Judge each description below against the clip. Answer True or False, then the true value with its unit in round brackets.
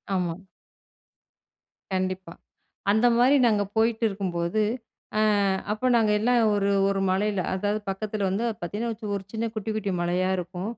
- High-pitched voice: True (205 Hz)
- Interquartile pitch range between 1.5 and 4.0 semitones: True (2.8 semitones)